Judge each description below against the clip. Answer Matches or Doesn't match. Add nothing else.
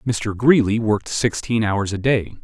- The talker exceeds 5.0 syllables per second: Doesn't match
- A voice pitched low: Matches